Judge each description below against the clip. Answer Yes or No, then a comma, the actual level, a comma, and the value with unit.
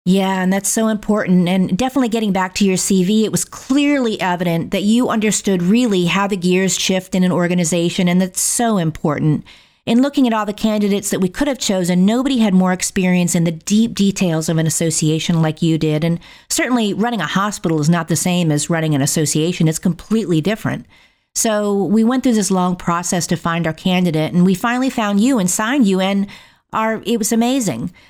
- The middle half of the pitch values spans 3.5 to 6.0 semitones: Yes, average, 3.8 semitones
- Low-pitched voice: No, high, 190 Hz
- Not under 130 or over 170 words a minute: No, fast, 205 wpm